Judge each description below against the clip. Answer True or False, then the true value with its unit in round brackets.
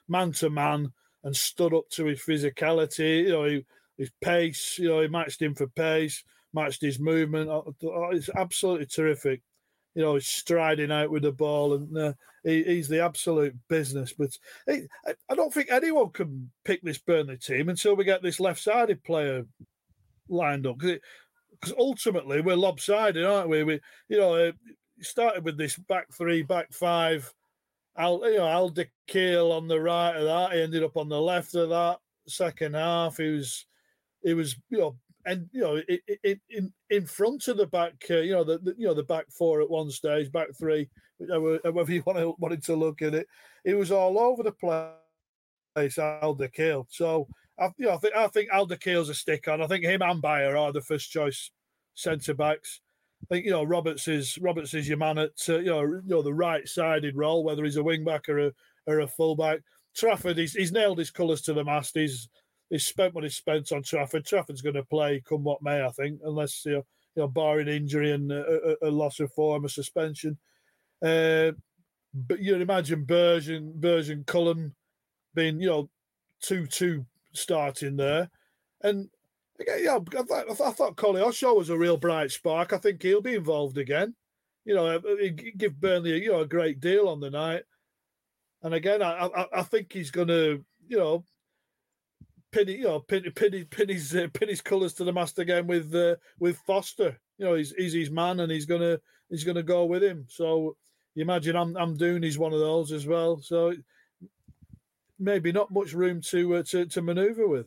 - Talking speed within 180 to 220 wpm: True (200 wpm)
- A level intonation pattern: False (3.1 semitones)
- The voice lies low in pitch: False (165 Hz)